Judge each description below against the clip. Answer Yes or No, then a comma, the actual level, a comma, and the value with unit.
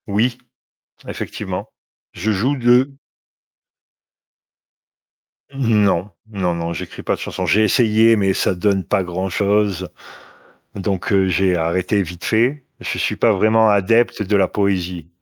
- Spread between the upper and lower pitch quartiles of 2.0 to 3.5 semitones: Yes, average, 3.2 semitones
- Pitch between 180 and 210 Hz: No, low, 100 Hz